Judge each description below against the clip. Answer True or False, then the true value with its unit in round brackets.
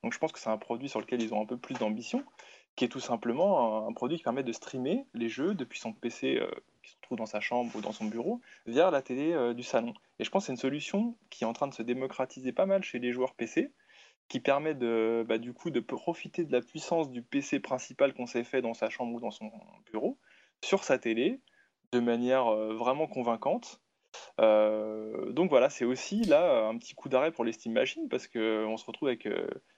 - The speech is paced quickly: True (240 wpm)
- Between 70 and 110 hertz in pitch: False (125 Hz)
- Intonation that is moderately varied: False (5.9 semitones)